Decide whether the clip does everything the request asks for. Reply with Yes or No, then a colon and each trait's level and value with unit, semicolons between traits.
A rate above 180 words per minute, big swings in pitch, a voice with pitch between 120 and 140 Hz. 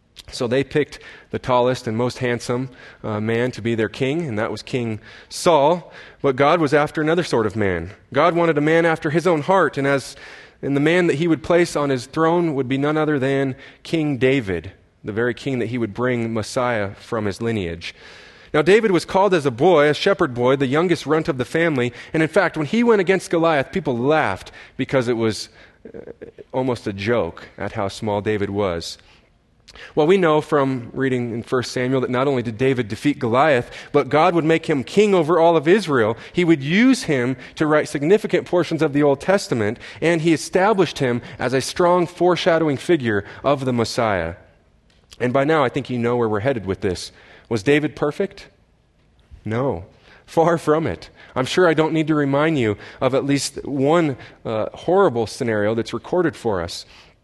Yes: average, 200 wpm; wide, 5.8 semitones; low, 135 Hz